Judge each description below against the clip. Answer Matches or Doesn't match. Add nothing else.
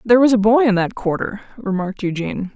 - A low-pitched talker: Doesn't match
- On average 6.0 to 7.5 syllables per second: Matches